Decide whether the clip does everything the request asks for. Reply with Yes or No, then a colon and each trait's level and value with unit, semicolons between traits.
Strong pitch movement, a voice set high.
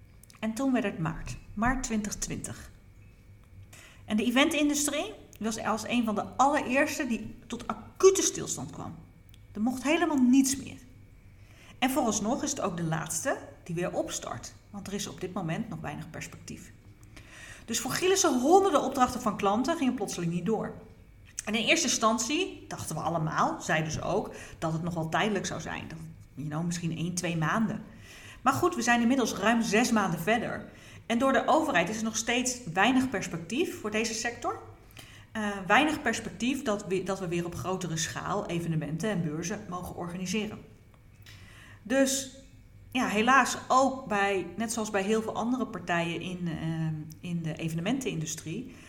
Yes: wide, 7.4 semitones; high, 205 Hz